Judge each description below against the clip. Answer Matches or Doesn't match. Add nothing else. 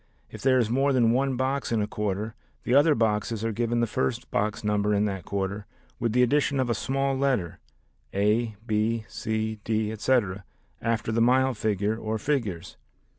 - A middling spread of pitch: Matches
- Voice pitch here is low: Matches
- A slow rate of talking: Doesn't match